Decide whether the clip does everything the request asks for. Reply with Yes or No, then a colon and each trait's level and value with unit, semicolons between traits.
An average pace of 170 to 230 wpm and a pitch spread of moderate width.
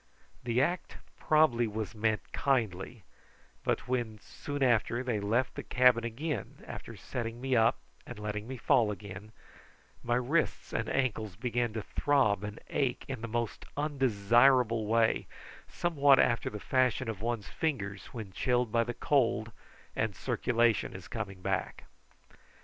No: average, 145 wpm; average, 3.1 semitones